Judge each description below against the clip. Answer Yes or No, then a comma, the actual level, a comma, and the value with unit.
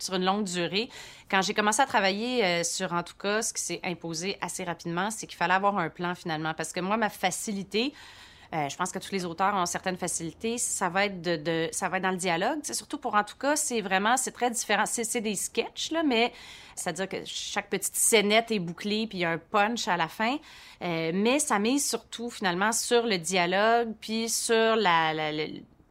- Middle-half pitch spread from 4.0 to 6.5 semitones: Yes, average, 4.3 semitones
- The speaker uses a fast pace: Yes, fast, 230 wpm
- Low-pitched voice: No, high, 195 Hz